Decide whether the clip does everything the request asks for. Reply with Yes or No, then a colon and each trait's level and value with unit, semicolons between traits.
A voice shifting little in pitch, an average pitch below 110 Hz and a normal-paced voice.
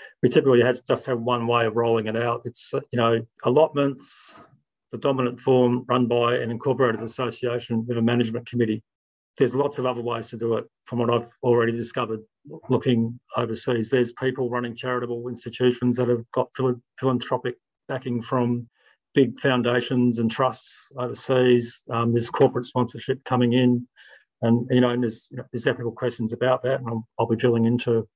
No: narrow, 1.3 semitones; low, 120 Hz; average, 175 wpm